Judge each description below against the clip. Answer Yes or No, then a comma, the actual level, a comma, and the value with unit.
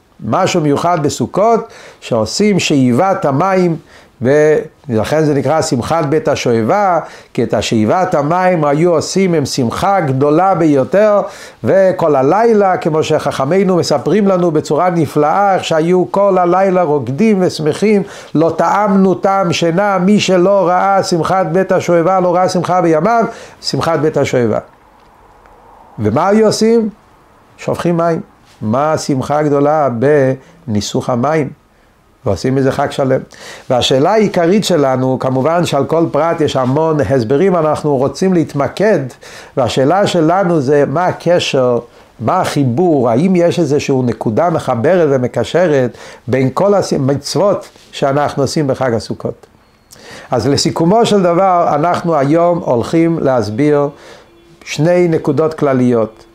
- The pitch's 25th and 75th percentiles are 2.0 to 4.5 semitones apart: No, average, 4.9 semitones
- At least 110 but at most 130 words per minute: Yes, average, 120 wpm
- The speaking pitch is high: No, medium, 155 Hz